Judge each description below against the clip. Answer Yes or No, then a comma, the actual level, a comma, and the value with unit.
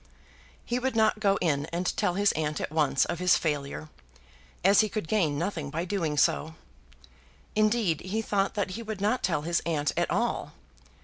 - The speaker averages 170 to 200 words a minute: Yes, average, 185 wpm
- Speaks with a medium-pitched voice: Yes, medium, 180 Hz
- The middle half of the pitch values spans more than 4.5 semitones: Yes, average, 5.2 semitones